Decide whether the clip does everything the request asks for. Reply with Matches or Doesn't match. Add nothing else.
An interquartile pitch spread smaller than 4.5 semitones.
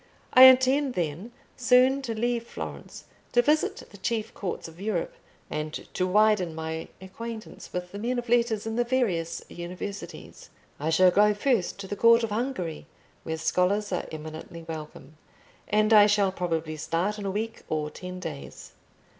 Doesn't match